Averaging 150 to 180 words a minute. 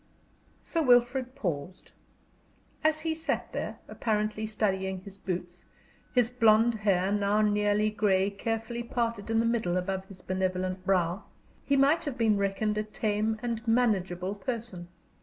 No: average, 140 wpm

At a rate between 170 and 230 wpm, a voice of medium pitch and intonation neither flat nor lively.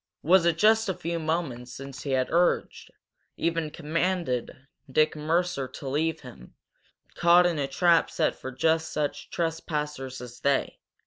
No: average, 150 wpm; medium, 155 Hz; average, 3.9 semitones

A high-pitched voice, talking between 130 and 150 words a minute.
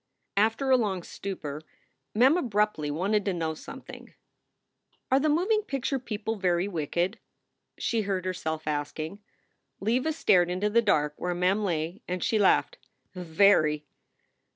Yes: high, 195 Hz; average, 140 wpm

